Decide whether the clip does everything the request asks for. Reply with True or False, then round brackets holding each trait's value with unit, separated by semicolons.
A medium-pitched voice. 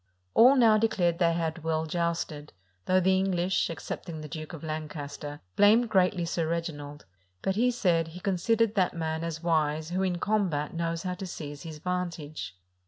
True (170 Hz)